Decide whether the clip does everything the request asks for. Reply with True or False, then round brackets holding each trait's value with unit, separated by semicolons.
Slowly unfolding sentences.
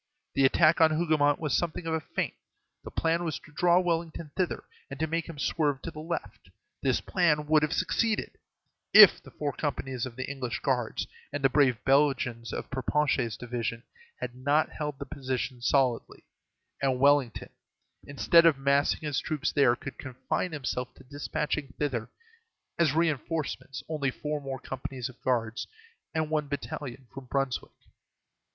False (160 wpm)